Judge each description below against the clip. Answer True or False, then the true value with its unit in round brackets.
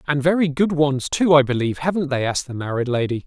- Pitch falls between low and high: True (145 Hz)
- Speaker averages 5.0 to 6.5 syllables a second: True (6.4 syllables/s)